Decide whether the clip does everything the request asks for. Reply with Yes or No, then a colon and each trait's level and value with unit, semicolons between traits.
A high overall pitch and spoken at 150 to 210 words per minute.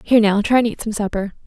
No: high, 215 Hz; fast, 285 wpm